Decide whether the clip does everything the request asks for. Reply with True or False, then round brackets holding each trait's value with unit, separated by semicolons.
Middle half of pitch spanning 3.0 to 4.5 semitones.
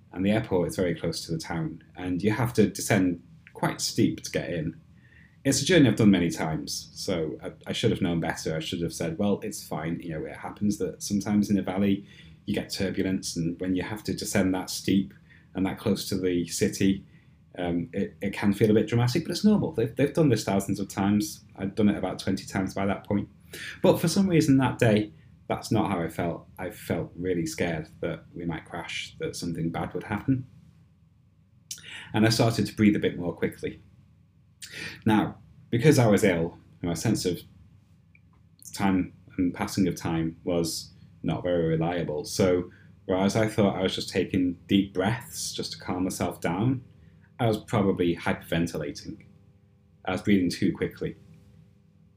True (3.4 semitones)